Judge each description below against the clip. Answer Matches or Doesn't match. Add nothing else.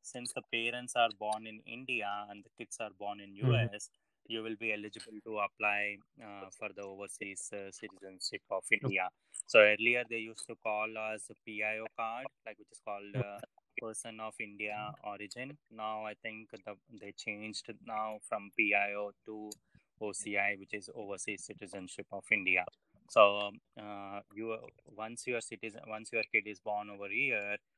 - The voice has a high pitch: Doesn't match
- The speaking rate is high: Matches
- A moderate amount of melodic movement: Doesn't match